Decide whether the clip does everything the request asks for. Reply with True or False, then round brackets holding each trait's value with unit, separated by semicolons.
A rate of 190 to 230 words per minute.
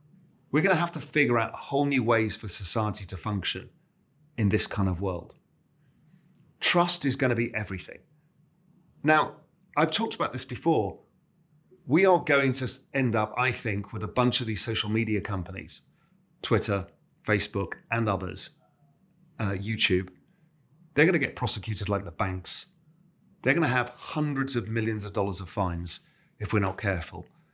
False (165 wpm)